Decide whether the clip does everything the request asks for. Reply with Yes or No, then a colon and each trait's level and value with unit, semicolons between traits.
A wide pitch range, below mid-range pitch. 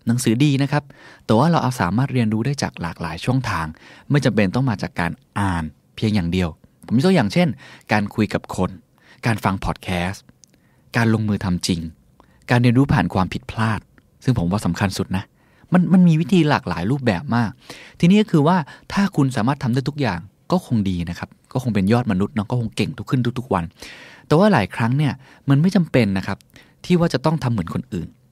Yes: wide, 6.6 semitones; low, 115 Hz